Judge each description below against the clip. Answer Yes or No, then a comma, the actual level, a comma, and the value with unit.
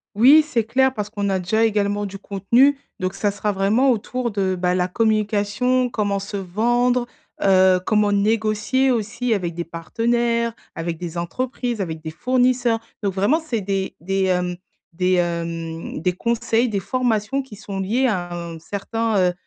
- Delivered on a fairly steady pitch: No, average, 4.2 semitones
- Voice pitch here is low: No, high, 205 Hz